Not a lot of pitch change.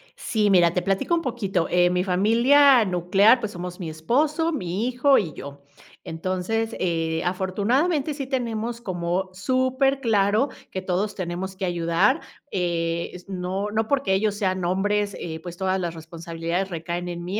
No: average, 4.5 semitones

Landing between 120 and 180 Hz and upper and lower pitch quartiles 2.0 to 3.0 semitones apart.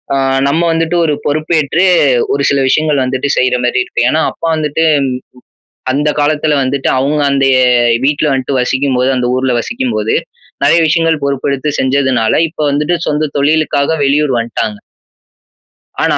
Yes: medium, 140 Hz; average, 2.7 semitones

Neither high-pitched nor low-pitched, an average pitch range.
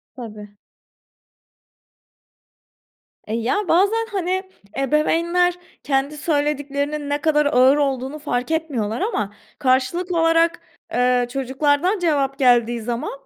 No: very high, 290 Hz; average, 4.7 semitones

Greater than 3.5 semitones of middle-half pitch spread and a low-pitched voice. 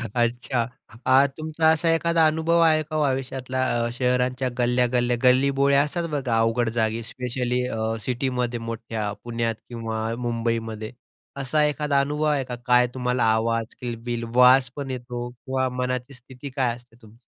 No: average, 2.7 semitones; low, 125 Hz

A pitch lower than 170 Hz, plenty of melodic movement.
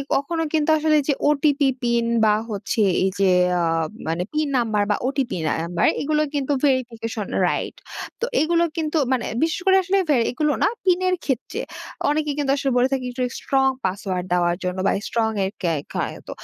No: very high, 265 Hz; wide, 6.3 semitones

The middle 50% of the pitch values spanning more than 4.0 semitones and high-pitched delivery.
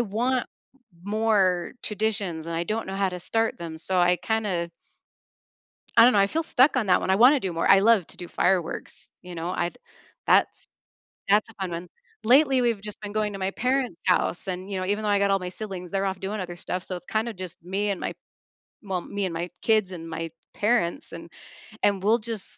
No: average, 3.6 semitones; high, 195 Hz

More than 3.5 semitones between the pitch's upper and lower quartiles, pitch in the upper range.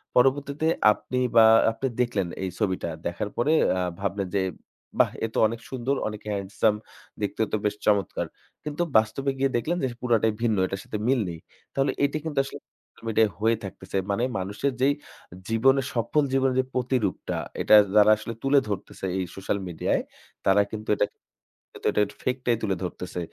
No: average, 4.7 semitones; low, 115 Hz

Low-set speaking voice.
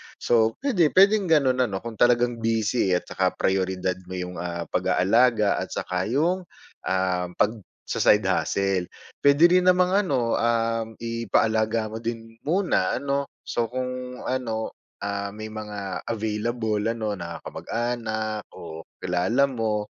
Yes: low, 115 Hz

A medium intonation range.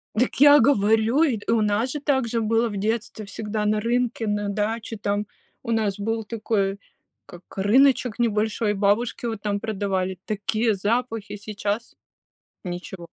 No: narrow, 2.3 semitones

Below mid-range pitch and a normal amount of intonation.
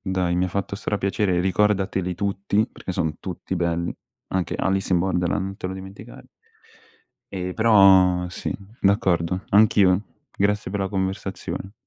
No: very low, 95 Hz; narrow, 1.6 semitones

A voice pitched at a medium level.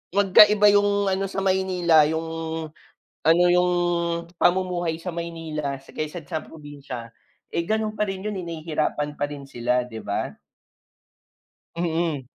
Yes: medium, 170 Hz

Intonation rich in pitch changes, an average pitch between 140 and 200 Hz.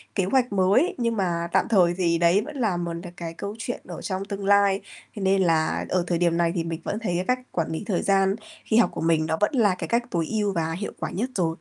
No: average, 3.4 semitones; high, 190 Hz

